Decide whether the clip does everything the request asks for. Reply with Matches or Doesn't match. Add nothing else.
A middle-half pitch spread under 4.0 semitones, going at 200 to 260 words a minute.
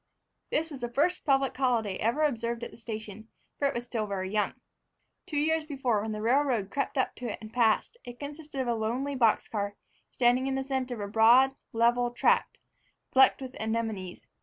Matches